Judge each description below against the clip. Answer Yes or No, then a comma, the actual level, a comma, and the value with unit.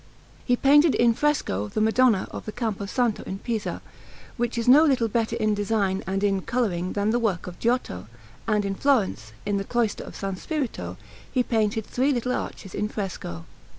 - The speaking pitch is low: No, high, 220 Hz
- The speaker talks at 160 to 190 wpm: Yes, average, 185 wpm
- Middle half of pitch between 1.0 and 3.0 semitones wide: No, average, 3.8 semitones